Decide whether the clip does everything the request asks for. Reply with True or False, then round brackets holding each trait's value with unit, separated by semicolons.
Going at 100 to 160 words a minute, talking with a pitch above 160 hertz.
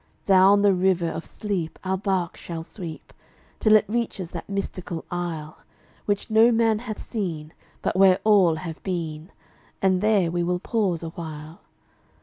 True (150 wpm; 185 Hz)